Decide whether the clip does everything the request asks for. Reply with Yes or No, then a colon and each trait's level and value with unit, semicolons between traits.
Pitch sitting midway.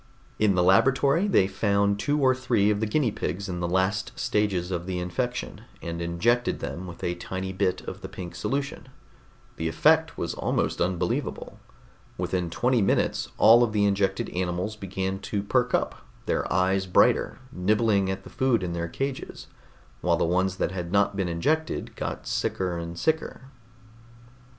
No: very low, 95 Hz